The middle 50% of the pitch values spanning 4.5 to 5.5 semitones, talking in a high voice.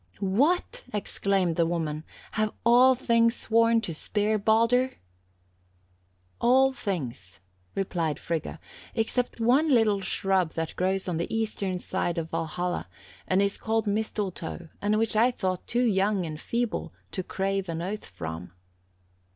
Yes: average, 4.8 semitones; high, 200 Hz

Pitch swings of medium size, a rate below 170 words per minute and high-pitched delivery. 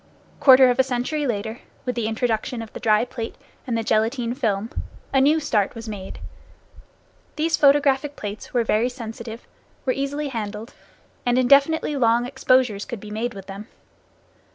Yes: average, 3.3 semitones; average, 160 wpm; high, 240 Hz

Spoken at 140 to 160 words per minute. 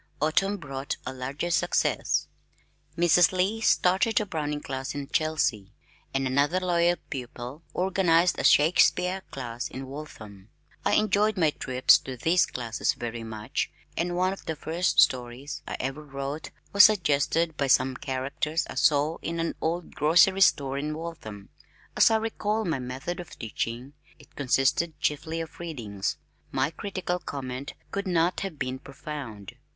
Yes: average, 150 wpm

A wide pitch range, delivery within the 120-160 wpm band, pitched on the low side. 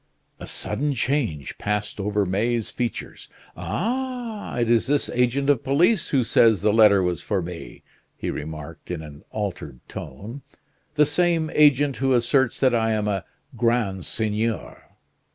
Yes: wide, 5.7 semitones; average, 150 wpm; low, 115 Hz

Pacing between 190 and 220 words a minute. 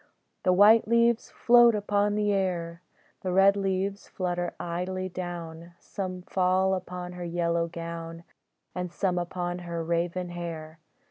No: slow, 135 wpm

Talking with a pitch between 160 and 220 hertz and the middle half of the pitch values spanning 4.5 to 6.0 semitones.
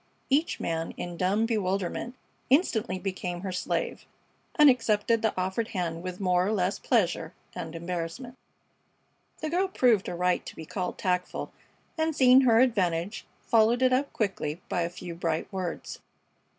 Yes: high, 190 Hz; average, 5.0 semitones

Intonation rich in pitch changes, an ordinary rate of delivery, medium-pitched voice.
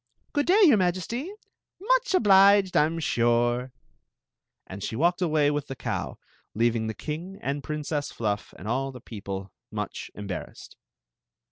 Yes: wide, 8.3 semitones; average, 145 wpm; medium, 150 Hz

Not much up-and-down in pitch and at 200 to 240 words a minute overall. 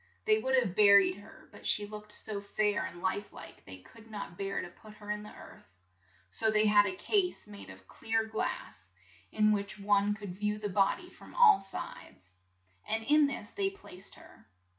Yes: narrow, 2.0 semitones; fast, 205 wpm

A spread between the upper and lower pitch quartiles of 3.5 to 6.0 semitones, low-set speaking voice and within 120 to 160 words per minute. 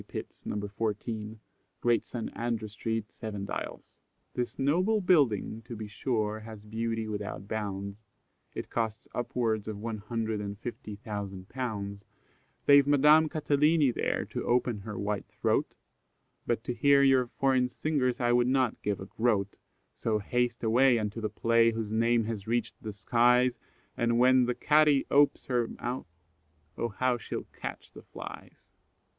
No: average, 2.9 semitones; low, 115 Hz; average, 155 wpm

